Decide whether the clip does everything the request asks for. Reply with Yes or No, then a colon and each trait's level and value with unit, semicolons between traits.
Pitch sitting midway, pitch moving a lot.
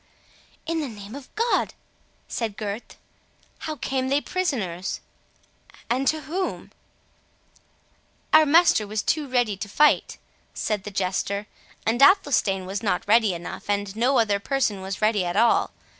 No: high, 225 Hz; wide, 5.7 semitones